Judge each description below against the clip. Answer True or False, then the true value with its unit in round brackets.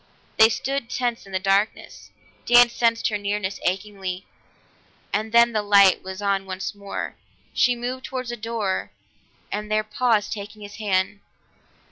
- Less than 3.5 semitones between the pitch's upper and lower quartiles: True (2.9 semitones)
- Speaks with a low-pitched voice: False (210 Hz)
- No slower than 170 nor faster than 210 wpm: False (150 wpm)